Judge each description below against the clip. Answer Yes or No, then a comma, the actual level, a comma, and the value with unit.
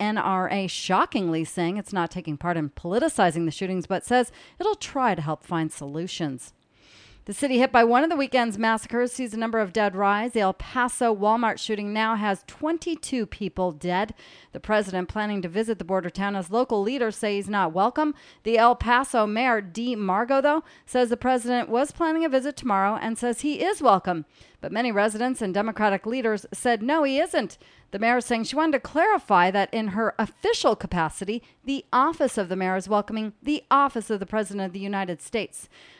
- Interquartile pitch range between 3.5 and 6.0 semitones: Yes, average, 4.3 semitones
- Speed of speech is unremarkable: Yes, average, 195 wpm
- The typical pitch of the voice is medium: No, high, 220 Hz